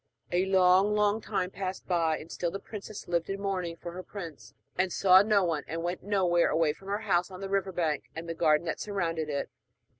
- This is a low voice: No, medium, 180 Hz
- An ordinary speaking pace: No, fast, 220 wpm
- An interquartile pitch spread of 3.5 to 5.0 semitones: No, average, 2.8 semitones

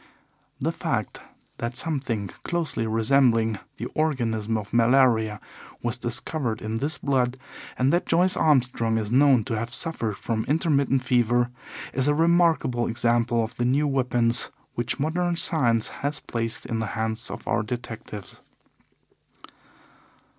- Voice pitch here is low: Yes, low, 120 Hz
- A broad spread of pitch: No, average, 3.7 semitones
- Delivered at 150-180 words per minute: No, slow, 135 wpm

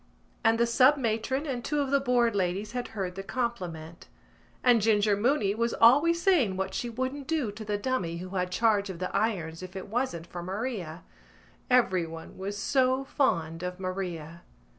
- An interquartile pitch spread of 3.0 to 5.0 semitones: No, wide, 5.5 semitones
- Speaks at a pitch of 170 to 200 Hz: No, high, 210 Hz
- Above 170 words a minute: Yes, average, 180 wpm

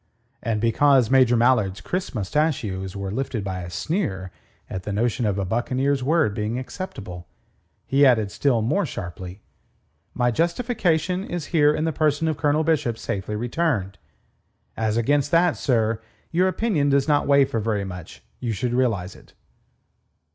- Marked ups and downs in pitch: Yes, wide, 6.4 semitones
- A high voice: No, low, 125 Hz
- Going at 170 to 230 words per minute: No, average, 155 wpm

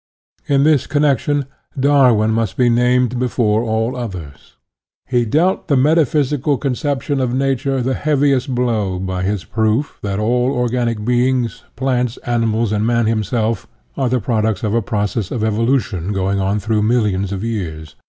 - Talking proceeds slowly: No, average, 160 wpm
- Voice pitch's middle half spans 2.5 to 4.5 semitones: Yes, average, 3.6 semitones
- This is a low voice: Yes, low, 120 Hz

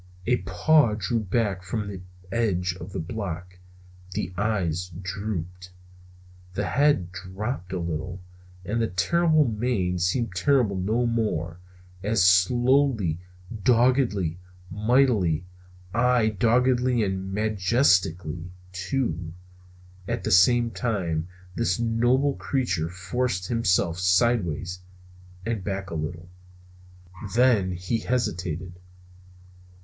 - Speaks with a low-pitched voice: Yes, low, 100 Hz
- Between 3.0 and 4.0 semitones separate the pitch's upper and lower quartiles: No, average, 4.7 semitones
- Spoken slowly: Yes, slow, 105 wpm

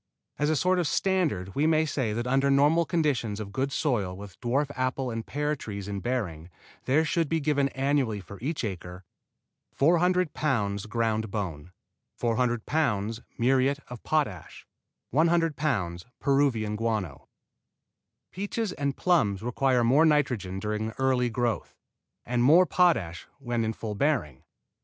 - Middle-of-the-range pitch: No, low, 125 Hz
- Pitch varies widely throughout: Yes, wide, 5.8 semitones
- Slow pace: No, average, 145 wpm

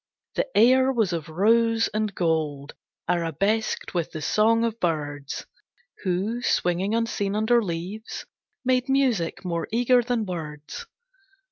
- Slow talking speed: Yes, slow, 125 wpm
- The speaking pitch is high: Yes, high, 205 Hz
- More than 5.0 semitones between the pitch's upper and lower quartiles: Yes, wide, 5.5 semitones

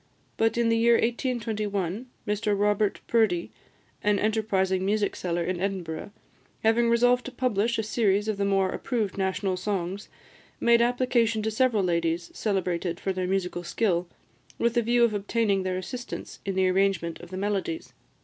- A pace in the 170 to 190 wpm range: No, average, 160 wpm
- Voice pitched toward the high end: Yes, high, 205 Hz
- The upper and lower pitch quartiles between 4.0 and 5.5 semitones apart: No, average, 3.5 semitones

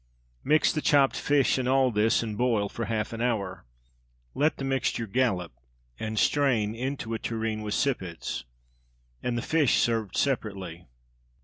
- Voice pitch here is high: No, low, 115 Hz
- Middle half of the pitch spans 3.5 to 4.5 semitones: Yes, average, 3.9 semitones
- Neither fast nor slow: Yes, average, 150 wpm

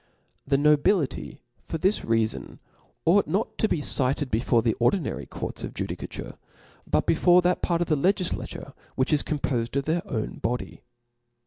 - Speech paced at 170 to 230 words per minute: No, average, 155 wpm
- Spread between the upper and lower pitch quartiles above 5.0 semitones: Yes, wide, 5.5 semitones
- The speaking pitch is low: No, medium, 150 Hz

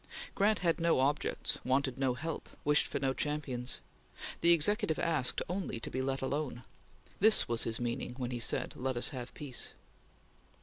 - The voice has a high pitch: No, low, 135 Hz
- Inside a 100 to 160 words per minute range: No, average, 170 wpm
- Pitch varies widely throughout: No, average, 4.5 semitones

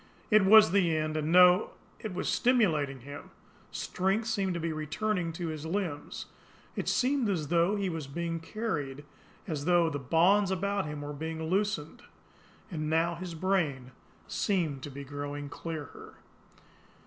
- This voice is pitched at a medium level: Yes, medium, 165 Hz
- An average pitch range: Yes, average, 4.3 semitones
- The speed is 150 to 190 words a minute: Yes, average, 155 wpm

